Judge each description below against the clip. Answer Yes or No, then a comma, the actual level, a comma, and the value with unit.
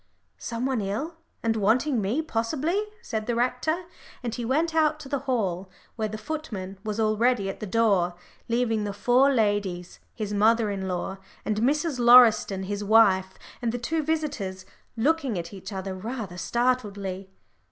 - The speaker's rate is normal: Yes, average, 165 wpm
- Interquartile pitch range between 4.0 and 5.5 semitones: Yes, average, 4.3 semitones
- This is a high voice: Yes, high, 225 Hz